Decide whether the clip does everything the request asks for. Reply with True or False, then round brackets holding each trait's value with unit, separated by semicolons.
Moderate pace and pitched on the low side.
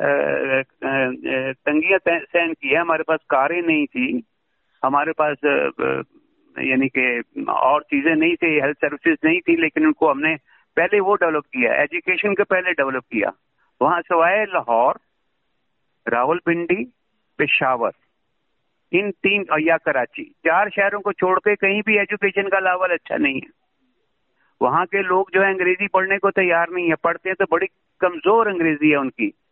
False (150 wpm; 185 Hz)